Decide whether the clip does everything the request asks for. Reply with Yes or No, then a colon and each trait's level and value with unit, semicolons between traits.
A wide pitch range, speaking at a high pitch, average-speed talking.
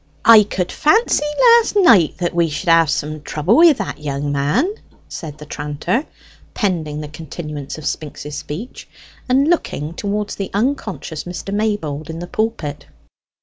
No: wide, 6.4 semitones; medium, 170 Hz; average, 150 wpm